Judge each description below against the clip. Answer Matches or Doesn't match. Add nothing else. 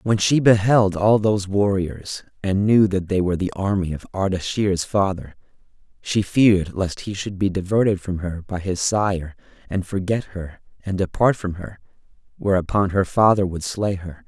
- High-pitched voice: Doesn't match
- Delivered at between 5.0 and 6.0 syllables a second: Doesn't match